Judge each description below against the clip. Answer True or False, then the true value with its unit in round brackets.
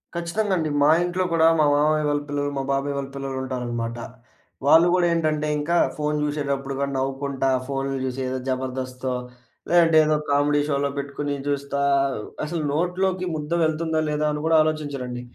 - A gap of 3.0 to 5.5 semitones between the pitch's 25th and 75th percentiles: False (2.5 semitones)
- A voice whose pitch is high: False (145 Hz)